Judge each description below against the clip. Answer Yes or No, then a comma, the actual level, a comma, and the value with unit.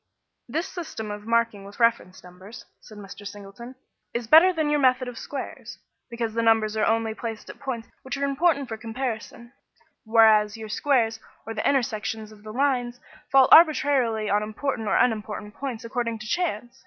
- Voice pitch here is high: Yes, high, 230 Hz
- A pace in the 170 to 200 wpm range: Yes, average, 175 wpm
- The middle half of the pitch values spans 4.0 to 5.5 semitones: No, average, 3.5 semitones